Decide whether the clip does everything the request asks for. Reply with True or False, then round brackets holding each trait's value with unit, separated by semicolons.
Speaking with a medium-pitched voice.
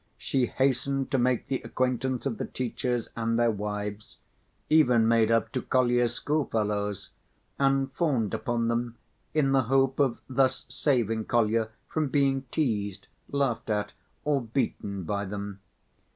False (120 Hz)